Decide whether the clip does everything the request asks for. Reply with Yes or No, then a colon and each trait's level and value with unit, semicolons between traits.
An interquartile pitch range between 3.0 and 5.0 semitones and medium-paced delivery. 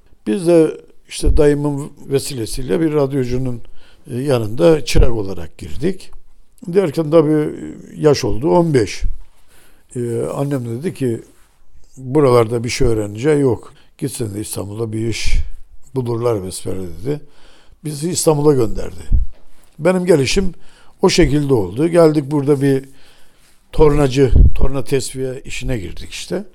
No: wide, 5.6 semitones; average, 115 wpm